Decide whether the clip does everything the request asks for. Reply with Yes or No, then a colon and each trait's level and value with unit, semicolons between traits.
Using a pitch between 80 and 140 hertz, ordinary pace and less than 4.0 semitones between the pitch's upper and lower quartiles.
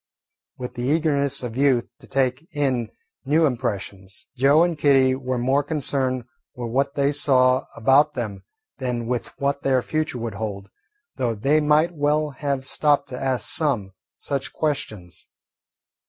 Yes: low, 135 Hz; average, 150 wpm; average, 2.9 semitones